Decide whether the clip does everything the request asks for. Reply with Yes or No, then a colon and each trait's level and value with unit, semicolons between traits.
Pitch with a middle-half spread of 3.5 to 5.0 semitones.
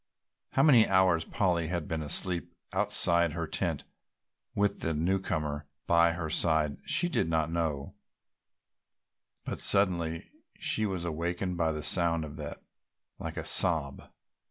No: average, 2.7 semitones